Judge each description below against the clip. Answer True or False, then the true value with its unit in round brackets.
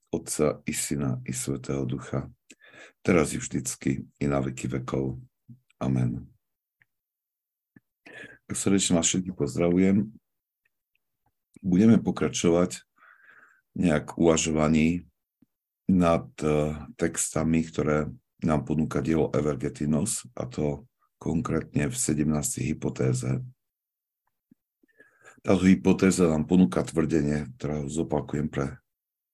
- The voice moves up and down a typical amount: True (3.5 semitones)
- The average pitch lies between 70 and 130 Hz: True (75 Hz)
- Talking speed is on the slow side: True (90 wpm)